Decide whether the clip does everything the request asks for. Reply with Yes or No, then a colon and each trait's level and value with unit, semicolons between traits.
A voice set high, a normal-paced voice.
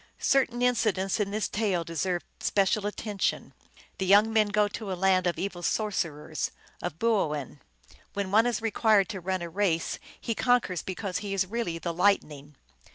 Yes: high, 195 Hz; average, 170 wpm